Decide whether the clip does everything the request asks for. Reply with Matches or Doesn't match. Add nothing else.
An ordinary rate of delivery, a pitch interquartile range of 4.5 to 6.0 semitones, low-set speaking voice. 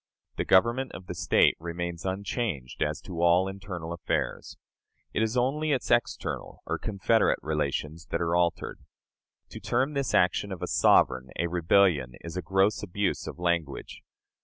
Doesn't match